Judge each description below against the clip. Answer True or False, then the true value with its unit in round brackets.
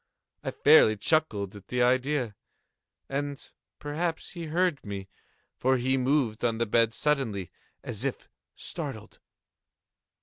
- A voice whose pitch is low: True (130 Hz)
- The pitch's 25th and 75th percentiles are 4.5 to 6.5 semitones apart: True (5.1 semitones)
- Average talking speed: False (125 wpm)